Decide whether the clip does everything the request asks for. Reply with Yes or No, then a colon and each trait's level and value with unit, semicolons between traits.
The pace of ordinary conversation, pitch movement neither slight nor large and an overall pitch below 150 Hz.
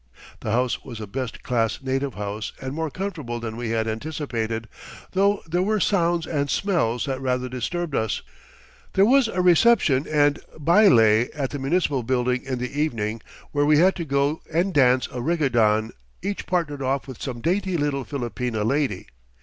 No: average, 175 wpm; wide, 5.7 semitones; low, 135 Hz